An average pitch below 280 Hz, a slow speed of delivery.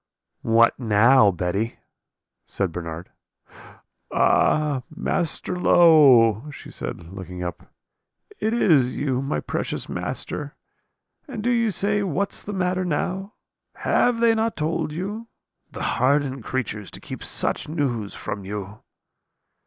Yes: medium, 140 Hz; slow, 120 wpm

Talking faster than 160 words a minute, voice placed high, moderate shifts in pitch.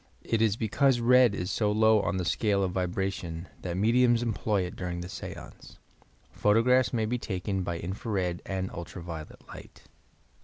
No: average, 180 wpm; low, 100 Hz; average, 4.0 semitones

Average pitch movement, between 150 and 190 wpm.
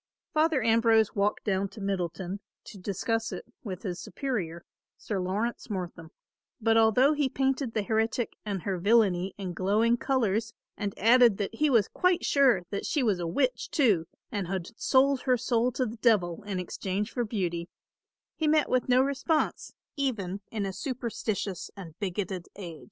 Yes: average, 4.7 semitones; average, 170 wpm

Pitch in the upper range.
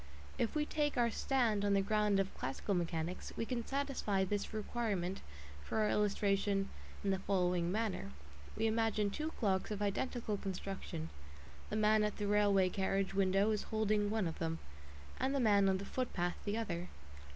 Yes: high, 205 Hz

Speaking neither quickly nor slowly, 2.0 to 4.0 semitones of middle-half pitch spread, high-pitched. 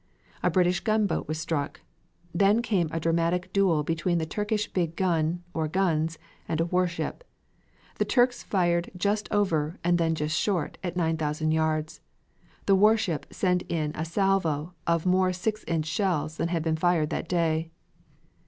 No: average, 160 wpm; average, 2.8 semitones; medium, 170 Hz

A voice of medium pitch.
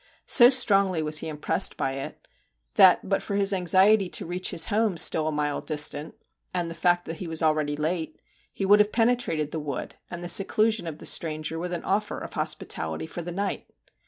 Yes: medium, 175 Hz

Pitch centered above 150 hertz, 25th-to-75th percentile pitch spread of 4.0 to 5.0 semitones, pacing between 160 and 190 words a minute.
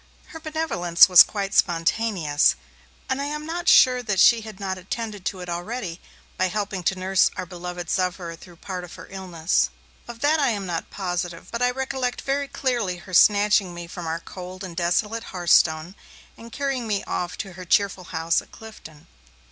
Yes: high, 190 Hz; average, 4.6 semitones; average, 185 wpm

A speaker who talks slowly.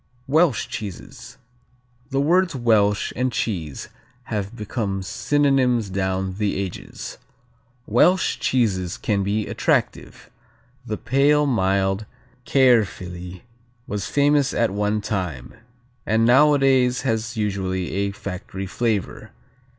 Yes: slow, 105 wpm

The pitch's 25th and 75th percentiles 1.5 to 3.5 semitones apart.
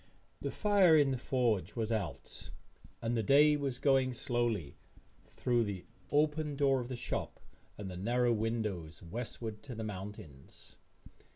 No: average, 4.5 semitones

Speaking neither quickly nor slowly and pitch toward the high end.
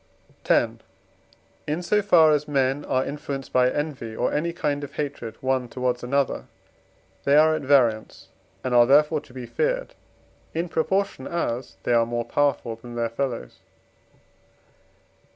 No: average, 150 wpm; medium, 140 Hz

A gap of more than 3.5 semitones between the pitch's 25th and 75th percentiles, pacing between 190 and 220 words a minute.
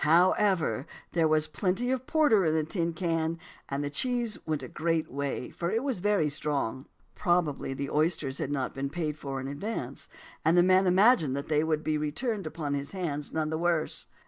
Yes: average, 4.2 semitones; average, 200 wpm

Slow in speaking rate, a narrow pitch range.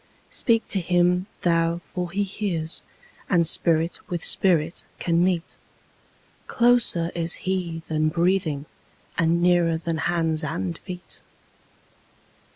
Yes: slow, 110 wpm; narrow, 1.7 semitones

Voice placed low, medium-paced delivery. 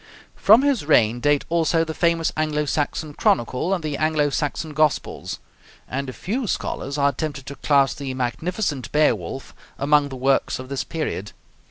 No: medium, 145 Hz; average, 165 wpm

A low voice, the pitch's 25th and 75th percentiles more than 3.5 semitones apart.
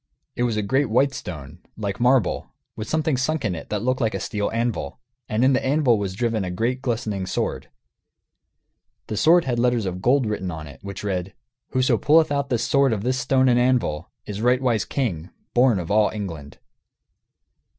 Yes: low, 115 Hz; average, 4.6 semitones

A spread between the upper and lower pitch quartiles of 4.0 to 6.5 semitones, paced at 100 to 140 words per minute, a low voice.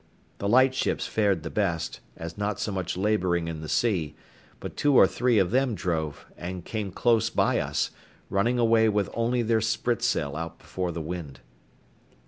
No: average, 5.2 semitones; average, 175 wpm; low, 100 Hz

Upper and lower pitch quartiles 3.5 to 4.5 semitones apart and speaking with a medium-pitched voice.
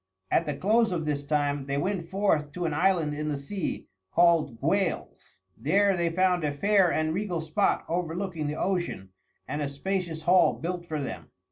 Yes: average, 3.9 semitones; medium, 165 Hz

